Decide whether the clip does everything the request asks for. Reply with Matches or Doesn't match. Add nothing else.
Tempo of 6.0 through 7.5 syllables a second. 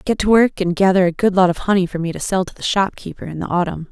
Matches